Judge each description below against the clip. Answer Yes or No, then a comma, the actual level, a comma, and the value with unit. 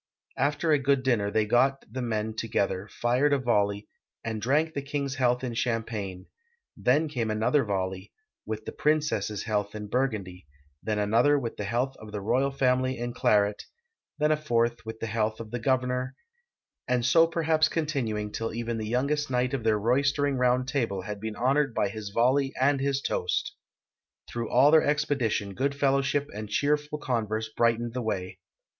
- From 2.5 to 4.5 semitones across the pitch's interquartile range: Yes, average, 4.2 semitones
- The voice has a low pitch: Yes, low, 120 Hz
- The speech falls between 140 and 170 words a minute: No, average, 185 wpm